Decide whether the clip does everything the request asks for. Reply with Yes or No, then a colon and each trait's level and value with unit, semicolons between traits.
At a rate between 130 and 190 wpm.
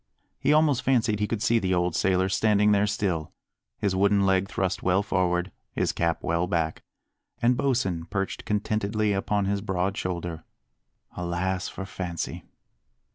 Yes: average, 150 wpm